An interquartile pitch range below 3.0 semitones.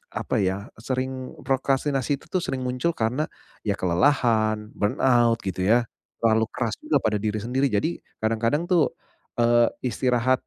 No: average, 3.3 semitones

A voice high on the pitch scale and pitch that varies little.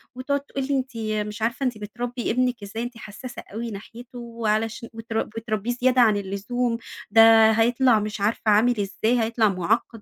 Yes: high, 230 Hz; narrow, 2.2 semitones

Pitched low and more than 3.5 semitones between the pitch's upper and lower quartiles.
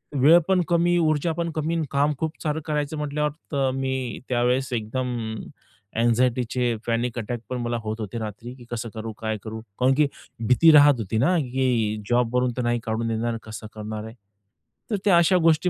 Yes: low, 125 Hz; average, 4.5 semitones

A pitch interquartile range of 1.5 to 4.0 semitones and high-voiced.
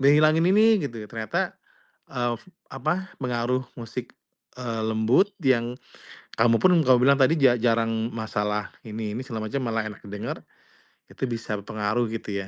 No: average, 2.9 semitones; low, 120 Hz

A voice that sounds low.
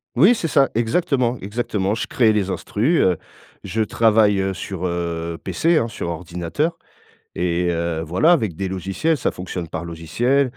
Yes: low, 100 Hz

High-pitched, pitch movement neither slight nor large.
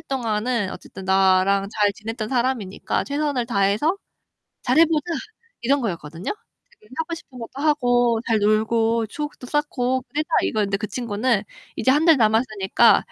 Yes: high, 230 Hz; average, 4.3 semitones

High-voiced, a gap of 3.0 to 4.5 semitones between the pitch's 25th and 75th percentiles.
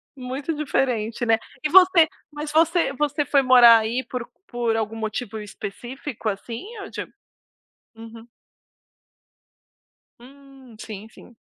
Yes: very high, 250 Hz; average, 4.2 semitones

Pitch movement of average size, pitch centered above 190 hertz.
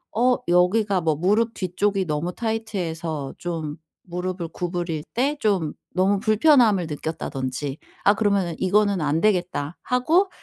No: average, 4.6 semitones; medium, 185 Hz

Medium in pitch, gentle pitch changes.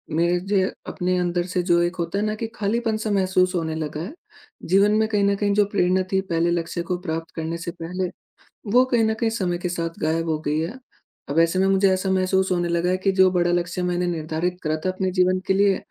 Yes: medium, 180 Hz; narrow, 2.3 semitones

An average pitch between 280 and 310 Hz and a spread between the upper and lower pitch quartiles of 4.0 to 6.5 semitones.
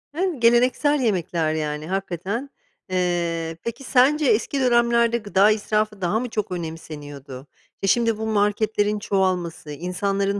No: high, 205 Hz; average, 5.2 semitones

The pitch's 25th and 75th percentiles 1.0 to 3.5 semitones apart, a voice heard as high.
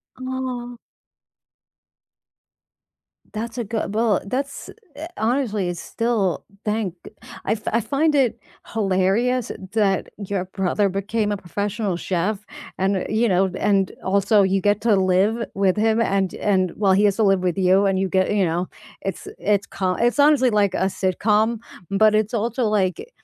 Yes: average, 3.1 semitones; high, 205 Hz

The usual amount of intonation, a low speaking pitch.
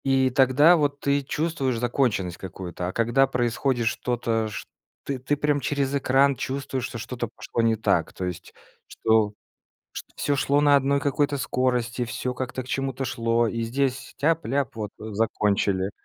Yes: average, 3.4 semitones; low, 130 Hz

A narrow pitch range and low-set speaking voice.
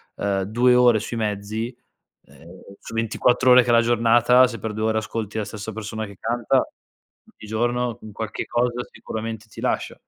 Yes: narrow, 1.9 semitones; low, 115 Hz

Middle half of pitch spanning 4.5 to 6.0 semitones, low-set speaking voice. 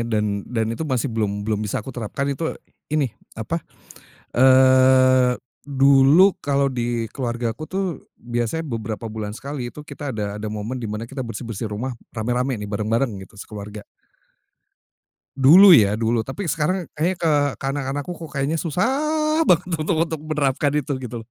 Yes: average, 5.0 semitones; low, 130 Hz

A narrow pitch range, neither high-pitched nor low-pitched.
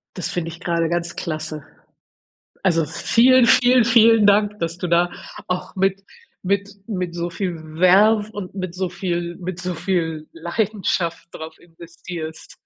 No: average, 3.0 semitones; medium, 180 Hz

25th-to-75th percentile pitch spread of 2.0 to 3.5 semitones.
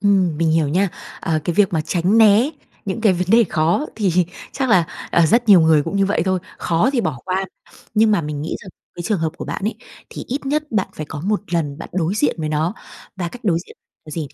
No: average, 4.6 semitones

